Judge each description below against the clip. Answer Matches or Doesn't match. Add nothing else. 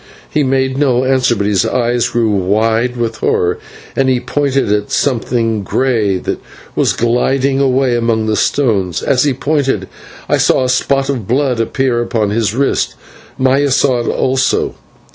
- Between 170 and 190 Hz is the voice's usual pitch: Doesn't match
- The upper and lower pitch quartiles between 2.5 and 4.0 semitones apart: Matches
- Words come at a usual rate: Matches